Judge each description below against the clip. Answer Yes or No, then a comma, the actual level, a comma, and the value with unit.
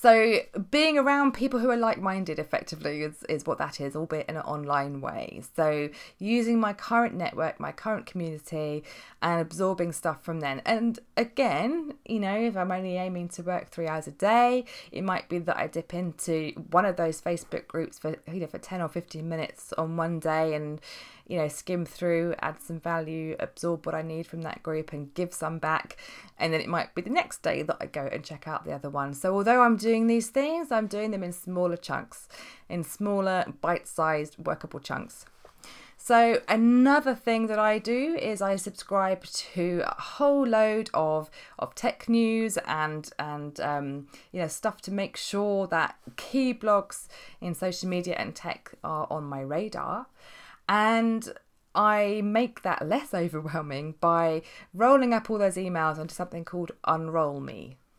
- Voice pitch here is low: No, medium, 180 Hz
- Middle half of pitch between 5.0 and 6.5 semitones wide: Yes, wide, 5.5 semitones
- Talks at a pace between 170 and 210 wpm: Yes, average, 180 wpm